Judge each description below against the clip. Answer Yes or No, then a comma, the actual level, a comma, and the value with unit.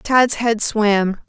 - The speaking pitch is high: Yes, high, 220 Hz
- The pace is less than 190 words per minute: Yes, average, 140 wpm